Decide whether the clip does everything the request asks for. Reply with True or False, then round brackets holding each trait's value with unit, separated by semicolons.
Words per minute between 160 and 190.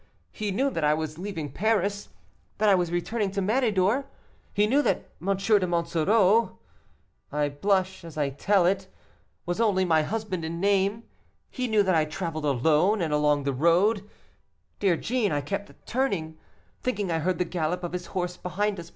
True (175 wpm)